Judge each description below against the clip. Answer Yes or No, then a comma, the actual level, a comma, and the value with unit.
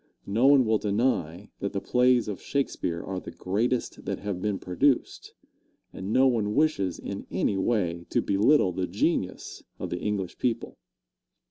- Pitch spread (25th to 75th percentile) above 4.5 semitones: Yes, average, 4.9 semitones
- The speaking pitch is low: Yes, low, 105 Hz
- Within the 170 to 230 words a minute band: No, average, 160 wpm